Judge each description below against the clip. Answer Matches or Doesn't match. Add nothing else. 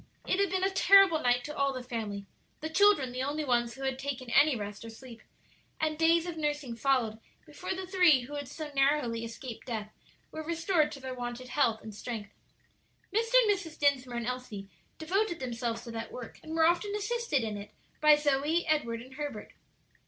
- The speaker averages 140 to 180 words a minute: Doesn't match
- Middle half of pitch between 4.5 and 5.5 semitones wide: Matches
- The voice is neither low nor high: Doesn't match